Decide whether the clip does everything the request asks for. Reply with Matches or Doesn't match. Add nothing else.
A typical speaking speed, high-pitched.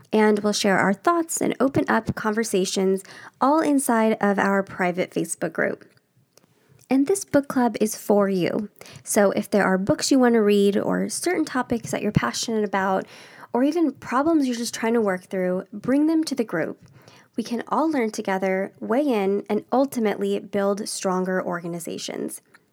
Matches